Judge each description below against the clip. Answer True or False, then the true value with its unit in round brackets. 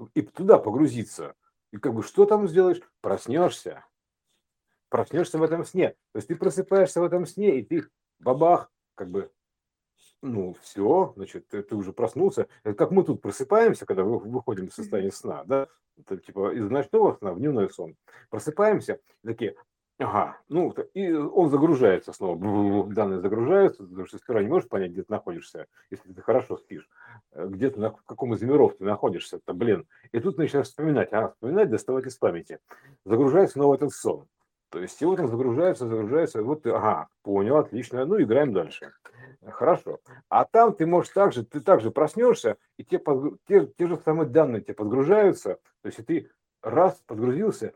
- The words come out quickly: True (170 wpm)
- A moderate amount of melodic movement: False (7.4 semitones)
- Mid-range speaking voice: True (170 Hz)